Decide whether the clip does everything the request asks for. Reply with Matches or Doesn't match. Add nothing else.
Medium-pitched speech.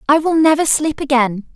Doesn't match